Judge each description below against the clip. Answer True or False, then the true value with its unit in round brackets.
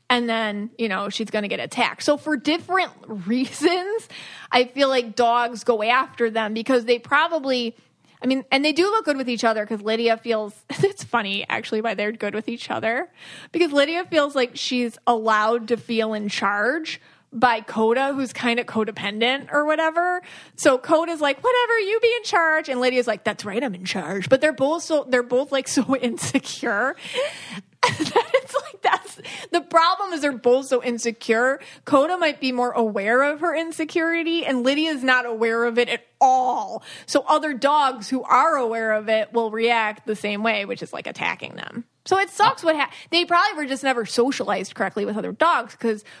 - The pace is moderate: True (195 wpm)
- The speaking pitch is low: False (255 Hz)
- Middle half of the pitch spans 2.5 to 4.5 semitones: False (5.5 semitones)